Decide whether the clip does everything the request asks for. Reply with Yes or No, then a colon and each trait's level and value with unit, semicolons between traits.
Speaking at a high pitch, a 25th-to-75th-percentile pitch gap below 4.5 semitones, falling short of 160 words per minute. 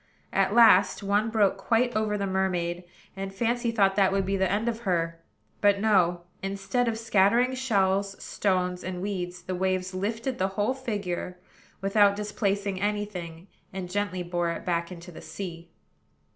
No: high, 195 Hz; narrow, 2.5 semitones; average, 165 wpm